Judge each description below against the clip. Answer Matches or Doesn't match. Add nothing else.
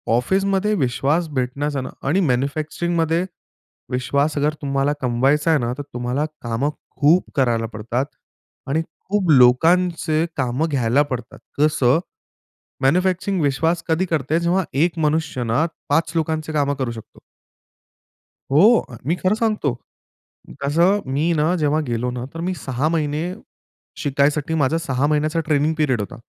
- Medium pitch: Matches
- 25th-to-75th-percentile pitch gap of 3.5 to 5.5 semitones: Matches